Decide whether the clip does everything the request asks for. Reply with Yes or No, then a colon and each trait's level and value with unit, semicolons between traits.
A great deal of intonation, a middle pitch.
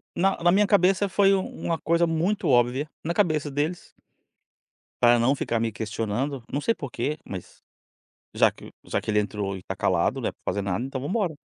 Yes: wide, 7.1 semitones; medium, 145 Hz